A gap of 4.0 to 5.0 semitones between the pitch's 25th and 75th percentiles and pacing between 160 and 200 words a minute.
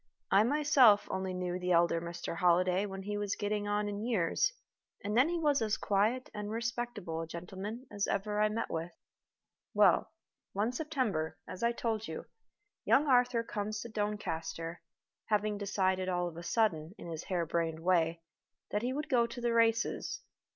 Yes: average, 4.5 semitones; average, 180 wpm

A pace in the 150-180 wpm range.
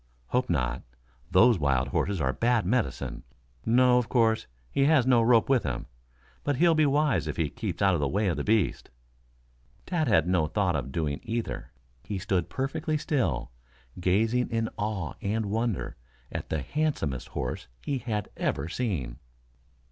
Yes: average, 165 wpm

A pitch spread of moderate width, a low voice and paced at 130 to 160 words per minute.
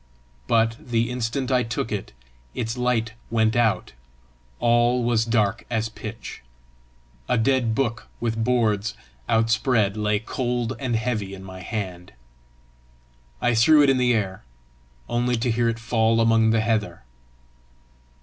No: narrow, 1.8 semitones; low, 115 Hz; average, 140 wpm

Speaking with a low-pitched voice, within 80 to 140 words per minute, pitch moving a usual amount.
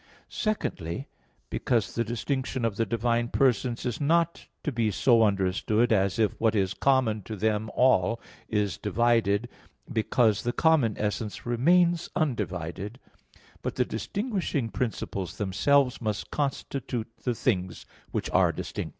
Yes: low, 115 Hz; slow, 135 wpm; average, 3.8 semitones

